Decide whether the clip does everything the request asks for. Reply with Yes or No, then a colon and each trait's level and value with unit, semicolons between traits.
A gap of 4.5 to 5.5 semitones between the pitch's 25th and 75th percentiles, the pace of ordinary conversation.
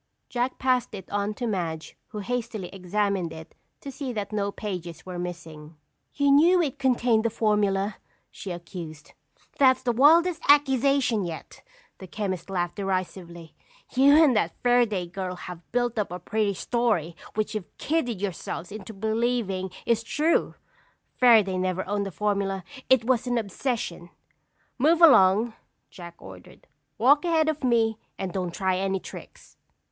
Yes: average, 5.1 semitones; average, 150 wpm